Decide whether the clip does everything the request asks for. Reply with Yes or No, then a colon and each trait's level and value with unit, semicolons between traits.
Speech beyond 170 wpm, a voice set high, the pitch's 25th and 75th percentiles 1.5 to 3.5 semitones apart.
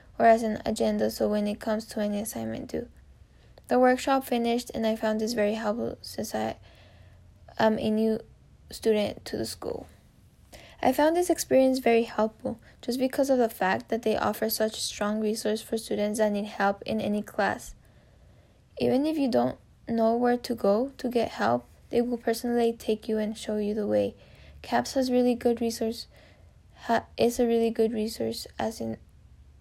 Yes: average, 180 wpm; high, 220 Hz; average, 3.2 semitones